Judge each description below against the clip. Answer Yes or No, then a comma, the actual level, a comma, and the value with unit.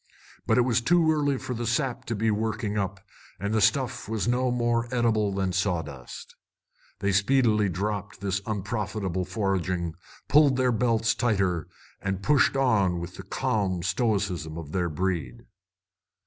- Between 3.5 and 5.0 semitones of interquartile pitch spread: Yes, average, 4.2 semitones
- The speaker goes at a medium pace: Yes, average, 150 wpm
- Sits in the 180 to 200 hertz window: No, low, 105 Hz